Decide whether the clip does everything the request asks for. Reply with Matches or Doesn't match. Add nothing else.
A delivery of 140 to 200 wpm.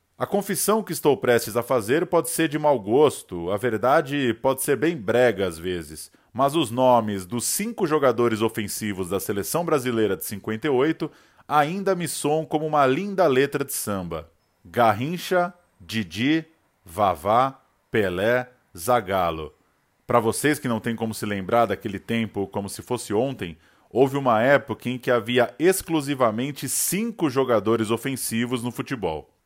Matches